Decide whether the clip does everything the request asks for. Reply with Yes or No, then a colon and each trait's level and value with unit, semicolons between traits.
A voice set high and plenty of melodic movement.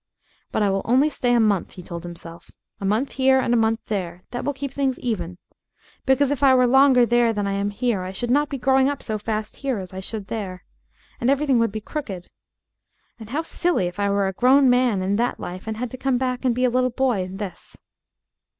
No: high, 235 Hz; average, 4.8 semitones